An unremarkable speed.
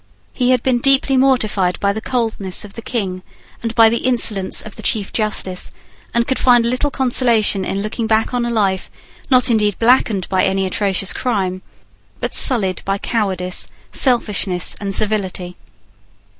Yes: average, 160 wpm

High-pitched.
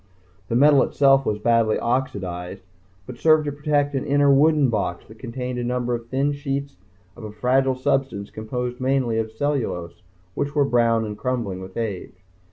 No: low, 125 Hz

